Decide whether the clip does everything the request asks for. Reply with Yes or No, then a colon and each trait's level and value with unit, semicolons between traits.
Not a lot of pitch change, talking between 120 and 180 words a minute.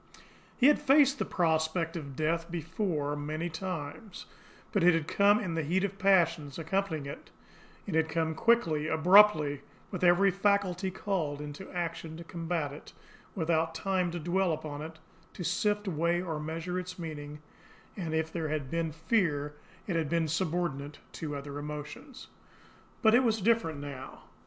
No: average, 3.5 semitones; average, 160 wpm